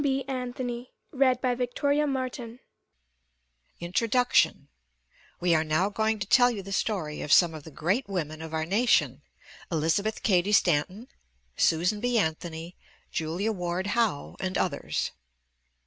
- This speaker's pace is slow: Yes, slow, 130 wpm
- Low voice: No, high, 190 Hz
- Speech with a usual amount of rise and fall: No, wide, 6.5 semitones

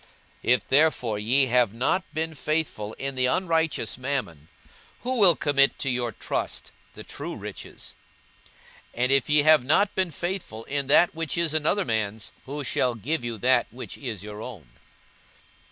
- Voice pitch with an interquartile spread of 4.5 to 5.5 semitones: Yes, average, 5.2 semitones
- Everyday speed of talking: Yes, average, 170 wpm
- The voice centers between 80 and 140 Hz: Yes, low, 135 Hz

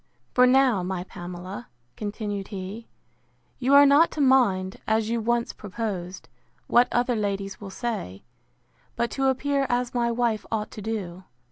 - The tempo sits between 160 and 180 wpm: No, average, 150 wpm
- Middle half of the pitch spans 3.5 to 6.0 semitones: Yes, average, 4.3 semitones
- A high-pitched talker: Yes, high, 220 Hz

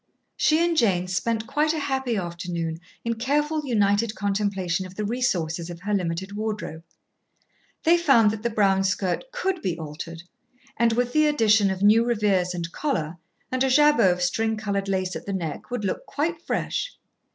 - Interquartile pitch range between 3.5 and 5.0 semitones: No, wide, 5.6 semitones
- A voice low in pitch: No, high, 210 Hz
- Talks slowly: No, average, 175 wpm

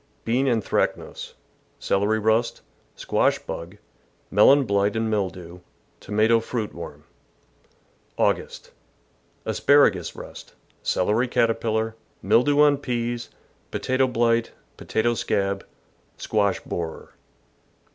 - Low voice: Yes, low, 110 Hz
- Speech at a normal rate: No, slow, 95 wpm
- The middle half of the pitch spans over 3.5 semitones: No, average, 3.0 semitones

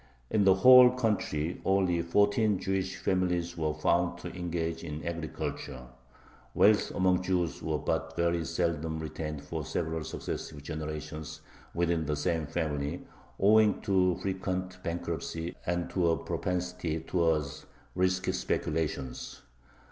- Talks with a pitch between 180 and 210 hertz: No, very low, 85 Hz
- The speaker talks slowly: Yes, slow, 125 wpm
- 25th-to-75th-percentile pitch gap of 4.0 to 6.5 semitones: No, average, 2.7 semitones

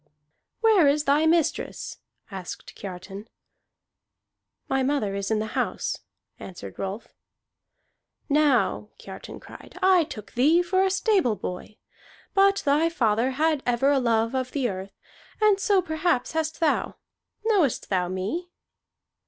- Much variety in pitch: Yes, wide, 7.9 semitones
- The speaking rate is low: Yes, slow, 130 wpm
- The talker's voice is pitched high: Yes, very high, 280 Hz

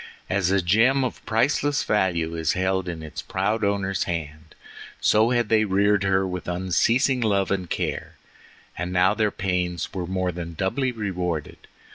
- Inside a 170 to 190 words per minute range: No, average, 160 wpm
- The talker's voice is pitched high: No, very low, 95 Hz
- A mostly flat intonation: No, average, 3.3 semitones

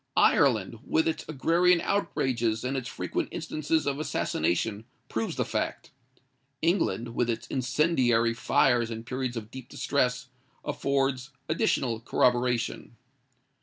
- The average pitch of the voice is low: Yes, low, 125 Hz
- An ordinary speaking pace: No, slow, 120 wpm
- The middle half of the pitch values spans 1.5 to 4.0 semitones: Yes, average, 3.7 semitones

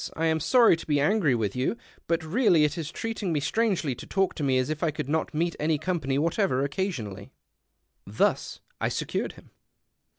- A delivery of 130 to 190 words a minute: No, average, 200 wpm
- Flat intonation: No, average, 4.6 semitones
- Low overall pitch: No, medium, 160 Hz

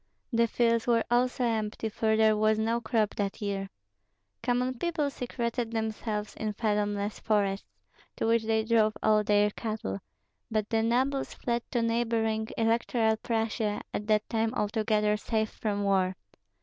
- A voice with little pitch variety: Yes, narrow, 1.7 semitones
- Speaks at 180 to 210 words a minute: No, average, 150 wpm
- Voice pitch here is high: Yes, high, 220 Hz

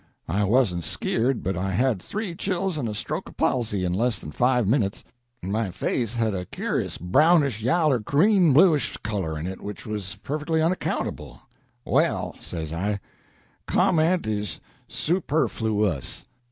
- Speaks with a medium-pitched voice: No, low, 115 Hz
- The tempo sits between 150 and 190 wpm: Yes, average, 155 wpm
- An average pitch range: No, wide, 7.8 semitones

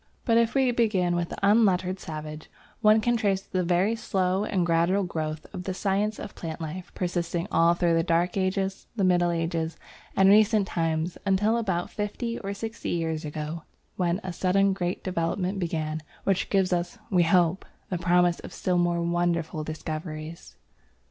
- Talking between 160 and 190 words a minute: Yes, average, 170 wpm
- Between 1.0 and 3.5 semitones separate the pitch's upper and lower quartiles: Yes, average, 2.7 semitones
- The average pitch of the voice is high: No, medium, 180 Hz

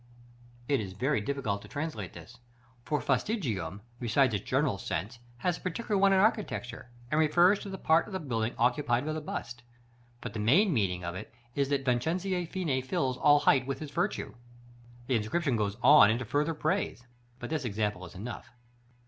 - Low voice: Yes, low, 130 Hz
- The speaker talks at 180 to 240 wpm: Yes, average, 185 wpm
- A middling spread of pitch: No, wide, 6.2 semitones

